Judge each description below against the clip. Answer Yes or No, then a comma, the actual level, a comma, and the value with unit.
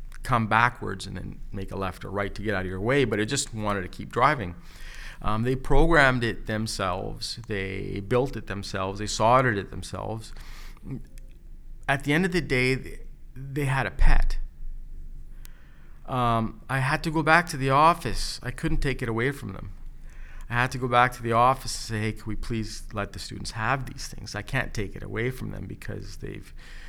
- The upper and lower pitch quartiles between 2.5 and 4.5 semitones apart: No, average, 5.0 semitones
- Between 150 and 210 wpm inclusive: Yes, average, 200 wpm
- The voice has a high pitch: No, low, 110 Hz